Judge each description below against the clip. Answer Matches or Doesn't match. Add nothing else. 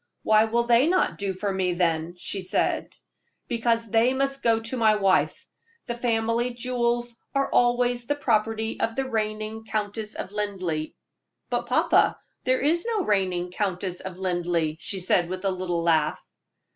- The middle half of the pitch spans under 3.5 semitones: Doesn't match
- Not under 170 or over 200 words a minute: Doesn't match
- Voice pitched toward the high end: Matches